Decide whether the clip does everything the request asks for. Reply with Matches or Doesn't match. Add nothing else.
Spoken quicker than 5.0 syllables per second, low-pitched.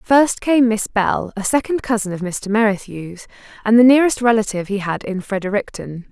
Doesn't match